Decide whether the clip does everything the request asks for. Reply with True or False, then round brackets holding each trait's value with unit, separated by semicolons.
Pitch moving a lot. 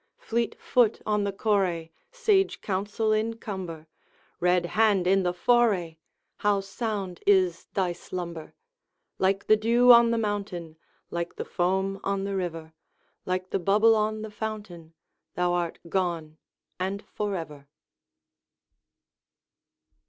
False (3.5 semitones)